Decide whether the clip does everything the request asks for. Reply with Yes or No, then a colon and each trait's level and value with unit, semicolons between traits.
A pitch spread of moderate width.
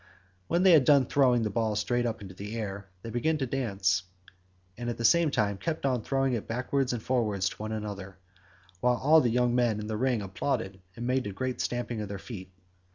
Yes: average, 3.9 semitones